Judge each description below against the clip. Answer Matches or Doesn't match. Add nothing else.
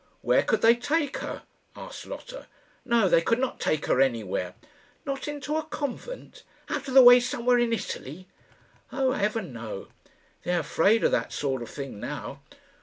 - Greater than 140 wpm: Matches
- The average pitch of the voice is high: Matches